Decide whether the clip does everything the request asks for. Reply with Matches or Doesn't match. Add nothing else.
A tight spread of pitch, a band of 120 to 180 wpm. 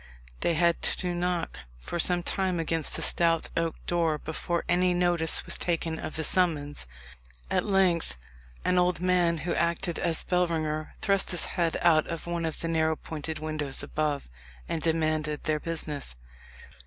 Matches